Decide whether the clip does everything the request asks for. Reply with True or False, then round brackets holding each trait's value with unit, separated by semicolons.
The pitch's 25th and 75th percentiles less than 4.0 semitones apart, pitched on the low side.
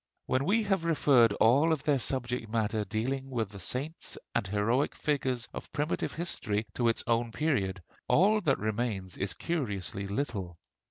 False (5.6 semitones; 120 Hz)